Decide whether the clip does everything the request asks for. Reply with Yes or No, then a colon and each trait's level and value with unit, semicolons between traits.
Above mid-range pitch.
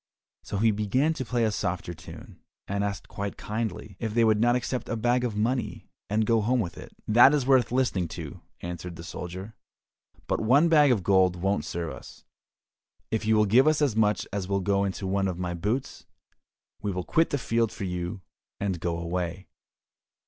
No: low, 105 Hz